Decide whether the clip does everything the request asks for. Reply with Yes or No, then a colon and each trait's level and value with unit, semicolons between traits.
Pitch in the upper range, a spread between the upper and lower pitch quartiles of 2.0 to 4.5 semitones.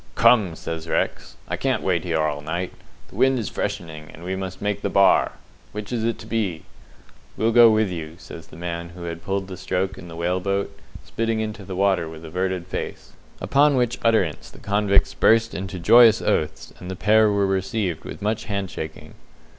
No: very low, 95 Hz; average, 4.1 semitones